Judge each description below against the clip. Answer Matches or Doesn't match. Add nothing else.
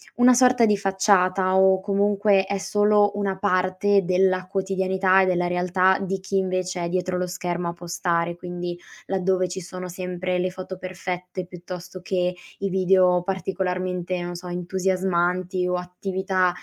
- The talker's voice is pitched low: Doesn't match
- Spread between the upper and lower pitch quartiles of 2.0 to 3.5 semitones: Doesn't match